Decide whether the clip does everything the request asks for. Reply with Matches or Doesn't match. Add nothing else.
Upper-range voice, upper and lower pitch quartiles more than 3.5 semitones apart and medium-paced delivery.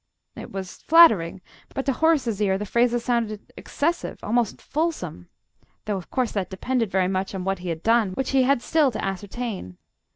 Matches